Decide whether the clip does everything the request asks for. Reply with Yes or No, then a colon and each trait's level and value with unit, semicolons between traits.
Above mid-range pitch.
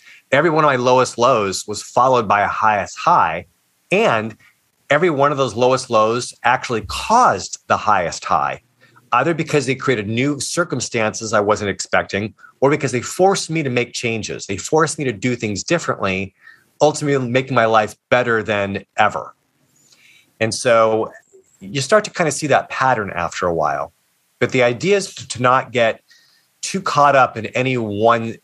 No: low, 125 Hz